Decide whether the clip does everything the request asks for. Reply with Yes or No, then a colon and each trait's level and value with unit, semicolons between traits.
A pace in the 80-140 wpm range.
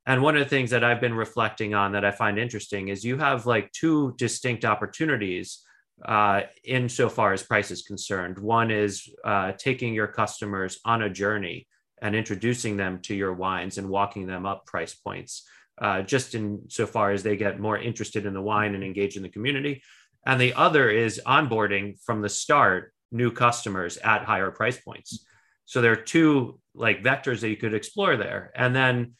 No: average, 195 wpm